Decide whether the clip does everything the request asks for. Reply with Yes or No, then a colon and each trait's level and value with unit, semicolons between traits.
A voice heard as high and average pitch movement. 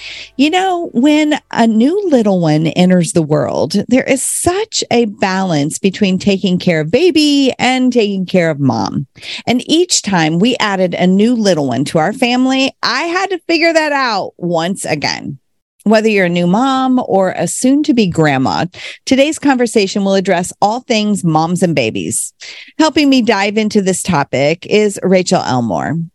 No: high, 205 Hz; wide, 6.9 semitones